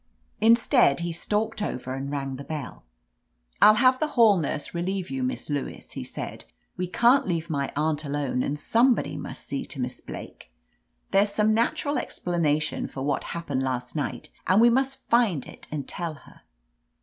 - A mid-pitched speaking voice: Yes, medium, 170 Hz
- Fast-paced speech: No, average, 175 wpm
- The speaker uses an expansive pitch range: Yes, wide, 7.8 semitones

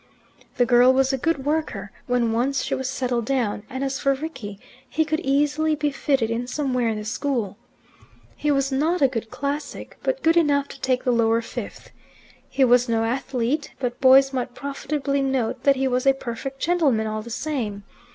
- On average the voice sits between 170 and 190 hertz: No, very high, 265 Hz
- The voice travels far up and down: No, average, 2.9 semitones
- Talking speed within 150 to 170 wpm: No, average, 190 wpm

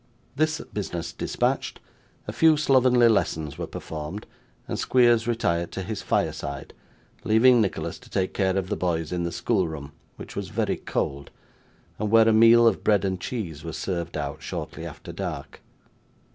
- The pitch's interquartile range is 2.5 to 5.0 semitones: No, wide, 5.5 semitones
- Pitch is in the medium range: No, very low, 95 Hz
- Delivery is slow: No, average, 165 wpm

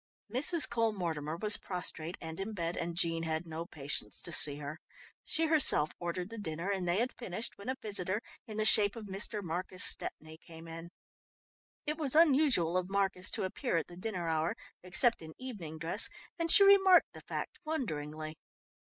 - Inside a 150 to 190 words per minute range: Yes, average, 185 wpm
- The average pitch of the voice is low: No, medium, 185 Hz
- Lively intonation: Yes, wide, 5.7 semitones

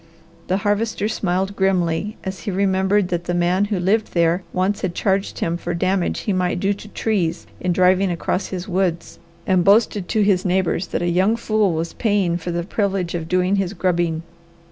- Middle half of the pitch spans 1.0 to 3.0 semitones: Yes, narrow, 2.4 semitones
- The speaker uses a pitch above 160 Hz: Yes, medium, 185 Hz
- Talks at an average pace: Yes, average, 190 wpm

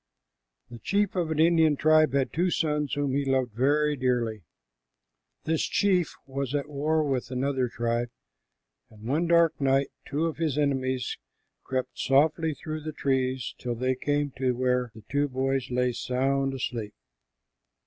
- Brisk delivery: No, average, 155 wpm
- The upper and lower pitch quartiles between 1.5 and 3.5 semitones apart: Yes, average, 3.0 semitones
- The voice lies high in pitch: No, low, 135 Hz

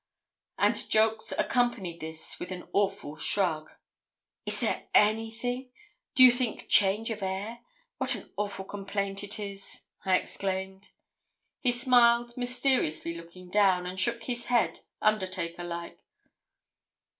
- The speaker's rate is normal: No, slow, 125 wpm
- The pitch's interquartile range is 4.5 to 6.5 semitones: No, average, 4.1 semitones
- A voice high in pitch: Yes, high, 200 Hz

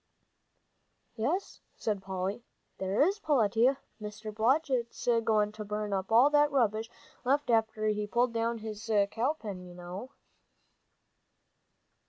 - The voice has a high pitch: Yes, high, 220 Hz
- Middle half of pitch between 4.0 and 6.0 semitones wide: No, average, 3.1 semitones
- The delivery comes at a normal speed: No, slow, 125 wpm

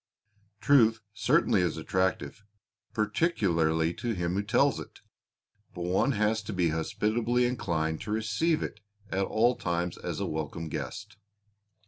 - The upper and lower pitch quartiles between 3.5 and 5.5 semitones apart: Yes, average, 4.6 semitones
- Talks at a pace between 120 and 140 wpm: Yes, slow, 135 wpm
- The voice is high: No, low, 100 Hz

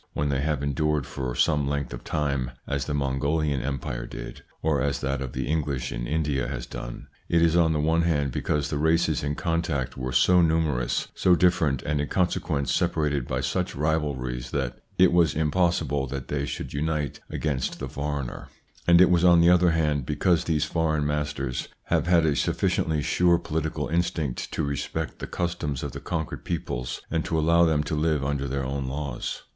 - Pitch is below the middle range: Yes, very low, 75 Hz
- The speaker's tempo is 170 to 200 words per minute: Yes, average, 190 wpm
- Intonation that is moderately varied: Yes, average, 3.0 semitones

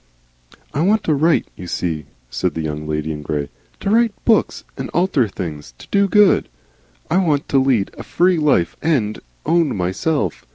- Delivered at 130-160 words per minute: No, average, 175 wpm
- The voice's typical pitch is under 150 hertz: Yes, low, 135 Hz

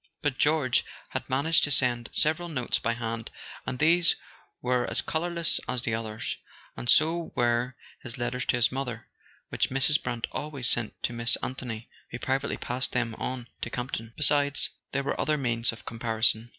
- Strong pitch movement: No, average, 3.4 semitones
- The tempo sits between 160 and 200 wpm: Yes, average, 175 wpm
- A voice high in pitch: No, low, 125 Hz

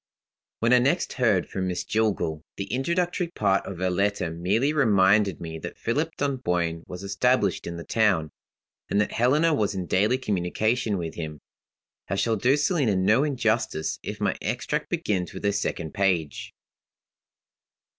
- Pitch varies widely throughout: Yes, wide, 5.7 semitones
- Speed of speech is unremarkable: Yes, average, 155 wpm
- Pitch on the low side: Yes, low, 100 Hz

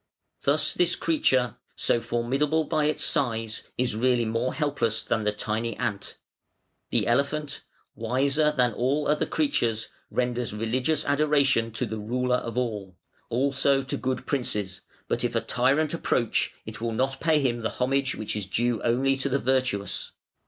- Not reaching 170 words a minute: Yes, average, 160 wpm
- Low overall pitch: Yes, low, 125 Hz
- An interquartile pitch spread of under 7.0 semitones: Yes, average, 3.6 semitones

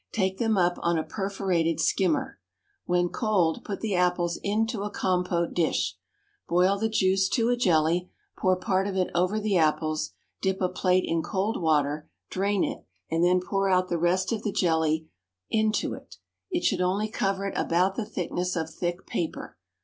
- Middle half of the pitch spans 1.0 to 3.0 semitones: Yes, narrow, 2.5 semitones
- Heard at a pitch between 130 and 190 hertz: Yes, medium, 185 Hz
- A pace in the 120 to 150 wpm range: No, average, 180 wpm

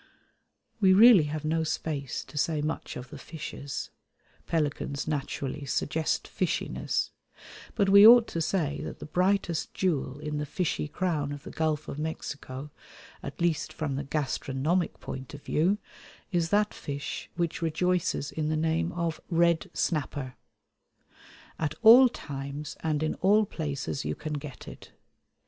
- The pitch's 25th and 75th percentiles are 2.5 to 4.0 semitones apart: Yes, average, 3.0 semitones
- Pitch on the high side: No, medium, 155 Hz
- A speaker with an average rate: Yes, average, 150 wpm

